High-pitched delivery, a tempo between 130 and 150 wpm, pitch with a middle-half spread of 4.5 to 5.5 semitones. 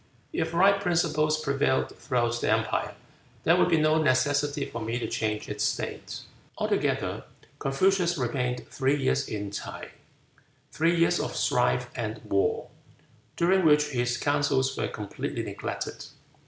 No: medium, 145 Hz; average, 140 wpm; average, 5.0 semitones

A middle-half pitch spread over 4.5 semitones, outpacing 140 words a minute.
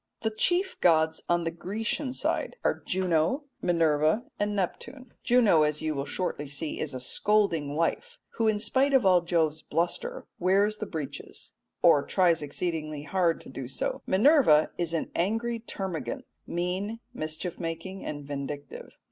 Yes: wide, 5.4 semitones; average, 155 wpm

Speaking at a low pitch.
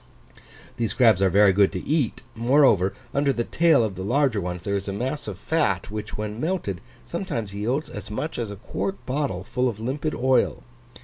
Yes: low, 115 Hz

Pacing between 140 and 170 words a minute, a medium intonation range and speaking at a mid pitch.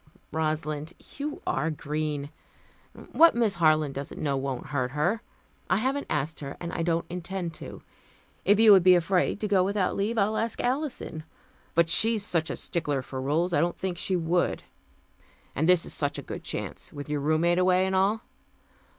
No: average, 185 wpm; average, 4.4 semitones; medium, 170 Hz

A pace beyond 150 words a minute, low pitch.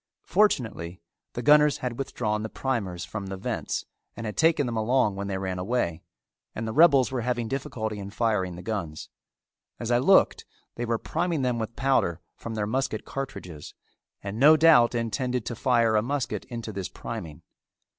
Yes: average, 175 wpm; low, 115 Hz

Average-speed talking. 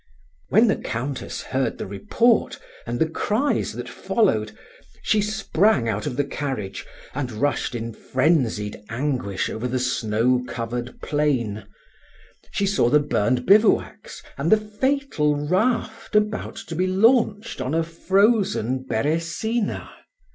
No: slow, 130 wpm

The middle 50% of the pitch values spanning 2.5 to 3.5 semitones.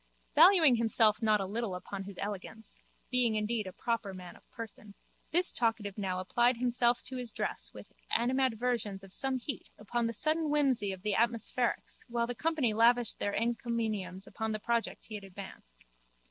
Yes: average, 3.1 semitones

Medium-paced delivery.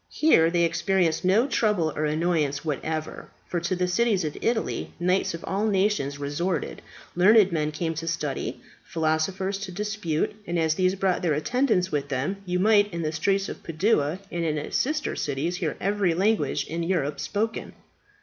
Yes: average, 170 wpm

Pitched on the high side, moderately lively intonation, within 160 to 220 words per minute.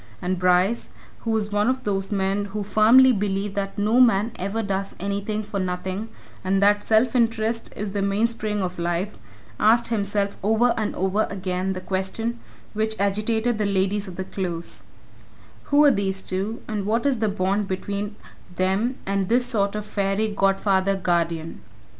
No: high, 200 Hz; narrow, 2.3 semitones; average, 165 wpm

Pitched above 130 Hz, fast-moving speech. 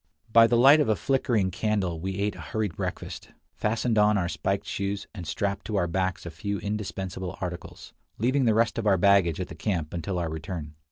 No: low, 100 Hz; fast, 210 wpm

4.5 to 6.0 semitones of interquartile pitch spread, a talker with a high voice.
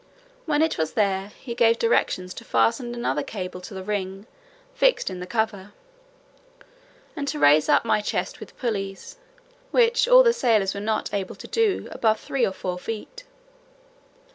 Yes: average, 5.2 semitones; high, 215 Hz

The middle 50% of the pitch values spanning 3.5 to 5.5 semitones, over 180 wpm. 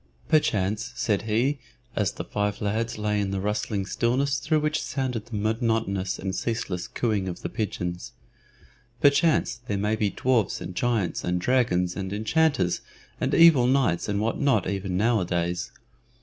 No: average, 4.0 semitones; average, 155 wpm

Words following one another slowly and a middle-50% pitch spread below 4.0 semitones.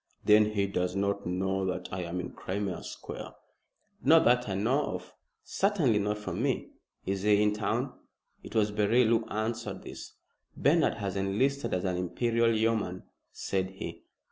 No: average, 165 wpm; average, 3.0 semitones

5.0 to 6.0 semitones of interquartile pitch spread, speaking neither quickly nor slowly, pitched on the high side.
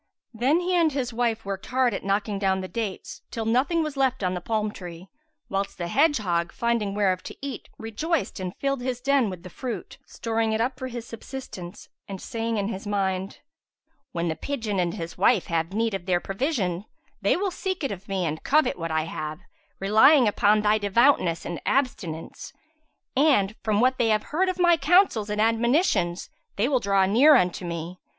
Yes: wide, 5.6 semitones; average, 195 wpm; high, 215 Hz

